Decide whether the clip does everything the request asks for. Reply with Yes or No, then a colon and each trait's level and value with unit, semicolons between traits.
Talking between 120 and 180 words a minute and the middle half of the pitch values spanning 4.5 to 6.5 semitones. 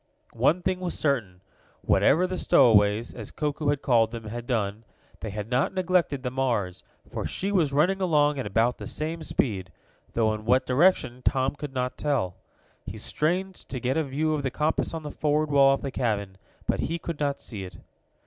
No: average, 195 wpm; average, 5.3 semitones